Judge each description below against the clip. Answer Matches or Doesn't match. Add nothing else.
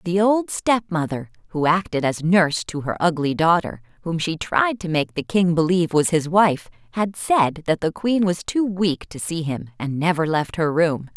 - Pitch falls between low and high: Matches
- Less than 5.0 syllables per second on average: Matches